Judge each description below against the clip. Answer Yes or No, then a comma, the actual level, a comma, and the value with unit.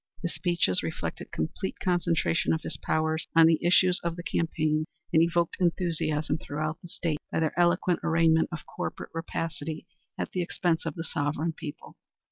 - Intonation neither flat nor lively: No, narrow, 1.7 semitones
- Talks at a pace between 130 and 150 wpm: No, average, 165 wpm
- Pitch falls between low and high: Yes, medium, 165 Hz